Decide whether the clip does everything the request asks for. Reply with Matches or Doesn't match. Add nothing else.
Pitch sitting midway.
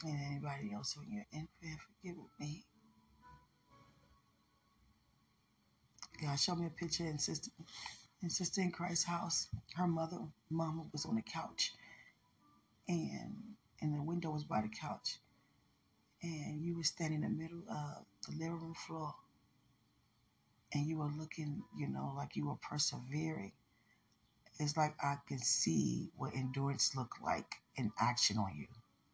Matches